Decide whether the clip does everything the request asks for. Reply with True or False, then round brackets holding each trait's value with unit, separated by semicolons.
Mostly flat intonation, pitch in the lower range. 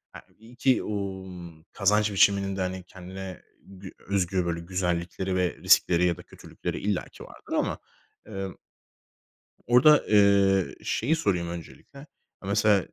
True (2.1 semitones; 95 Hz)